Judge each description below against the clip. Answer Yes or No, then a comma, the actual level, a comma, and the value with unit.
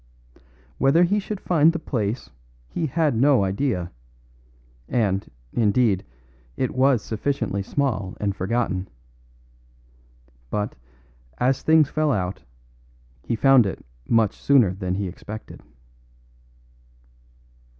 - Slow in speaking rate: Yes, slow, 105 wpm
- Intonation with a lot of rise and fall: Yes, wide, 6.1 semitones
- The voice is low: Yes, low, 115 Hz